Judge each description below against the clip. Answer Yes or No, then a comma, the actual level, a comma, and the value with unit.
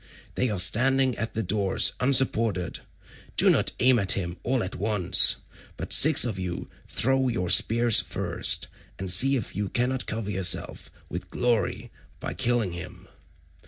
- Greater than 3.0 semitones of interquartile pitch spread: Yes, average, 4.9 semitones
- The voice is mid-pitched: No, low, 110 Hz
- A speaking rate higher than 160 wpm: No, average, 155 wpm